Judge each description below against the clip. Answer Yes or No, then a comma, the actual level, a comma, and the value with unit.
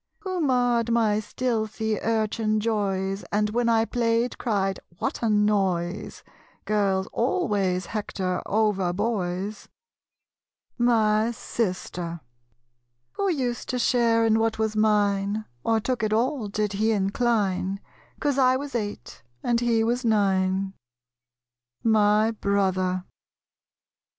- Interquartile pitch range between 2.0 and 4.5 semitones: Yes, average, 2.8 semitones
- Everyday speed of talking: No, slow, 115 wpm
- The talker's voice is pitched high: Yes, high, 215 Hz